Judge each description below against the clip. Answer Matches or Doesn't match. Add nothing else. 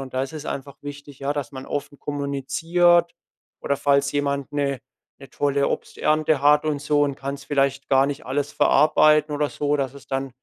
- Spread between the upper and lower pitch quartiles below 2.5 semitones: Matches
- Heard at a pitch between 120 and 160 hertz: Matches